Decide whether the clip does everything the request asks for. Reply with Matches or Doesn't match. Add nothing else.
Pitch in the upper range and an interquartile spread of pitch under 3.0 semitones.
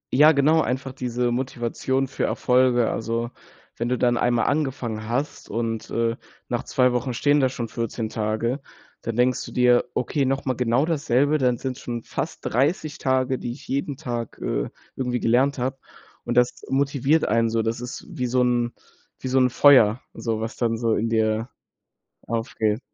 Doesn't match